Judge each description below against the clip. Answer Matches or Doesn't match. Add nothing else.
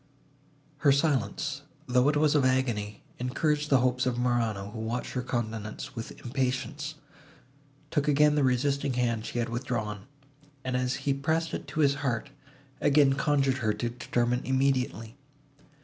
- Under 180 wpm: Matches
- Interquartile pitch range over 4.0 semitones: Doesn't match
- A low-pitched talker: Matches